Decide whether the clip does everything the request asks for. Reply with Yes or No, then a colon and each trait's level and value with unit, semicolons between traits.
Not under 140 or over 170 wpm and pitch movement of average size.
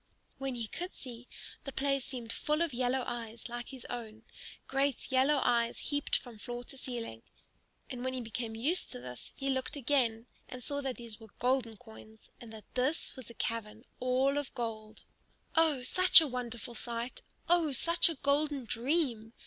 No: average, 180 wpm; average, 3.1 semitones